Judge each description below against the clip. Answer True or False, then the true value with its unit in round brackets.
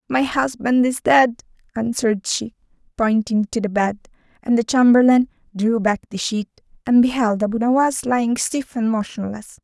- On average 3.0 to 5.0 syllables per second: True (4.9 syllables/s)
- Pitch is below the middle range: False (230 Hz)